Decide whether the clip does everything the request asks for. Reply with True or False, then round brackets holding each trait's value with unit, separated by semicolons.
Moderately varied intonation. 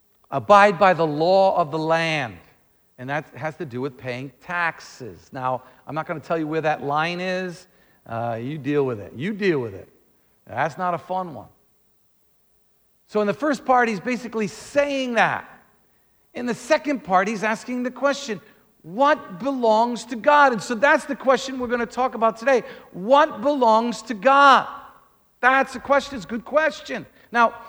False (7.9 semitones)